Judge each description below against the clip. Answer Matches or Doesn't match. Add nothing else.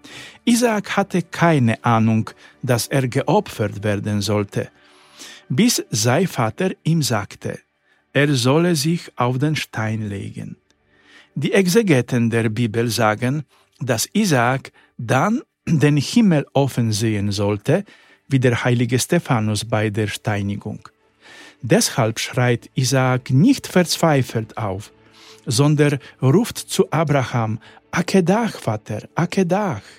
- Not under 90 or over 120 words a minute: Matches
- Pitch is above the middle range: Doesn't match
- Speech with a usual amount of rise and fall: Doesn't match